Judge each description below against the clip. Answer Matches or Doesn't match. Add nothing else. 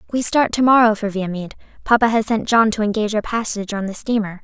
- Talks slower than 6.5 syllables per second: Doesn't match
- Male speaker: Doesn't match